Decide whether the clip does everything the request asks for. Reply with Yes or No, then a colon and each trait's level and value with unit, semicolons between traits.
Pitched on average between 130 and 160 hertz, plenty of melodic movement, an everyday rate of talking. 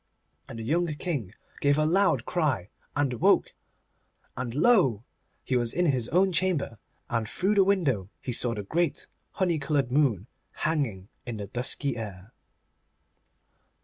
Yes: low, 135 Hz; wide, 6.9 semitones; average, 145 wpm